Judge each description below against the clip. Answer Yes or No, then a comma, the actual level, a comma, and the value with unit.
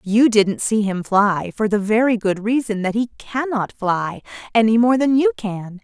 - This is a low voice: No, high, 220 Hz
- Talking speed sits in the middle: Yes, average, 195 wpm